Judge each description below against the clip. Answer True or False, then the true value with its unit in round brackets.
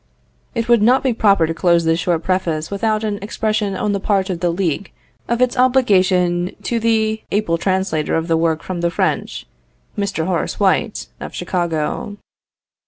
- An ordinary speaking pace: True (170 wpm)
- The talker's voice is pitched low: False (190 Hz)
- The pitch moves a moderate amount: True (4.1 semitones)